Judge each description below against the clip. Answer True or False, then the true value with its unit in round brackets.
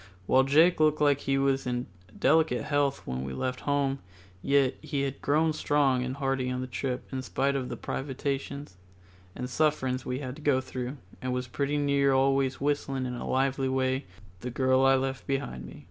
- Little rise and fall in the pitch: True (1.6 semitones)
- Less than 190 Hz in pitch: True (135 Hz)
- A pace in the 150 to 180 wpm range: False (190 wpm)